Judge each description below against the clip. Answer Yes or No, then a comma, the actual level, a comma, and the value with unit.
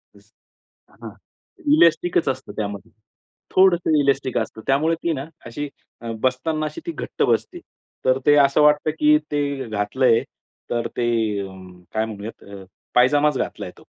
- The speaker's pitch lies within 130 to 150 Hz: Yes, medium, 140 Hz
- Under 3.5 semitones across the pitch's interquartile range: No, average, 4.5 semitones